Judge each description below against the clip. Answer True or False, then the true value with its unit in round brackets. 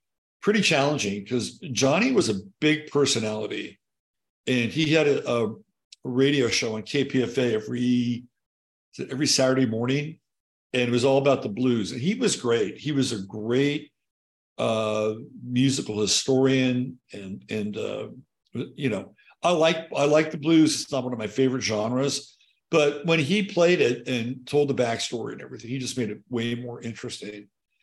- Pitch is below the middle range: True (130 Hz)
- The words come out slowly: False (160 wpm)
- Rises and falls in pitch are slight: False (3.7 semitones)